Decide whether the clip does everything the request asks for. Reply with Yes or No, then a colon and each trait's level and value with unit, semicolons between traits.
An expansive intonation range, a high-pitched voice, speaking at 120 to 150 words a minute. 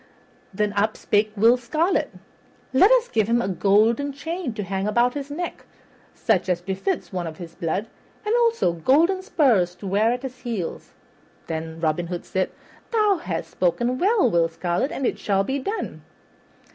No: wide, 7.6 semitones; high, 220 Hz; average, 170 wpm